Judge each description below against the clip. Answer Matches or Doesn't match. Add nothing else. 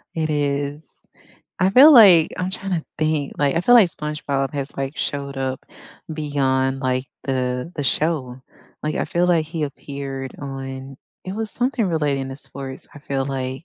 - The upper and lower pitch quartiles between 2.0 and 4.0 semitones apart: Matches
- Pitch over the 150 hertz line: Doesn't match